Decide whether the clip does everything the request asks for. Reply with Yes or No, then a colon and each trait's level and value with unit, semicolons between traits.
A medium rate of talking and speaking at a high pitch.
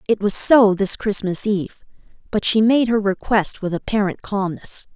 Yes: average, 170 wpm; high, 205 Hz